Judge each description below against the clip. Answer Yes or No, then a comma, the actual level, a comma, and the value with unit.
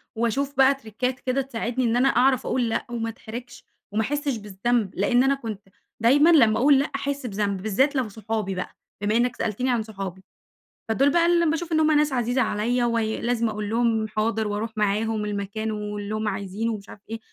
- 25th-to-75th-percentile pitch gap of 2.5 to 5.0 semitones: Yes, average, 3.7 semitones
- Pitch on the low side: No, high, 230 Hz